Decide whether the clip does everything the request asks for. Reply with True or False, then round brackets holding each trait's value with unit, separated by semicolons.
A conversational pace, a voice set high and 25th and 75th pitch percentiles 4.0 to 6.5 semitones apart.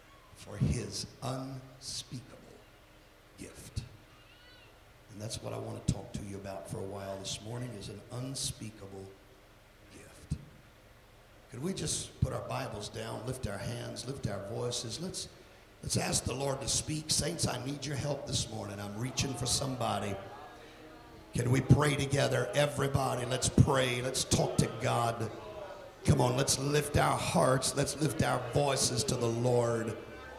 False (155 wpm; 125 Hz; 4.3 semitones)